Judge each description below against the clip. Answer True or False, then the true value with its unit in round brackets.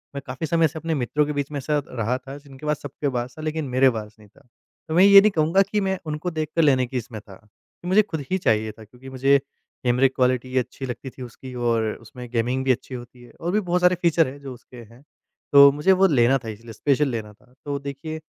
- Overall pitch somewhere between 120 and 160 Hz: True (135 Hz)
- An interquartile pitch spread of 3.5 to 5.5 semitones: True (4.0 semitones)